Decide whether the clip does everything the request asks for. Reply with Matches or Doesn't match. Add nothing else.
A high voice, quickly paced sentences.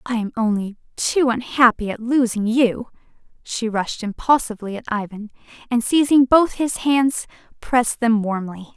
Doesn't match